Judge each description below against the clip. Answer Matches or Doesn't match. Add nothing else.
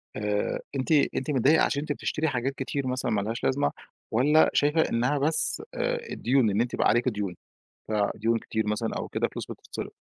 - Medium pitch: Doesn't match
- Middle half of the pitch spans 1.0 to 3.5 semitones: Doesn't match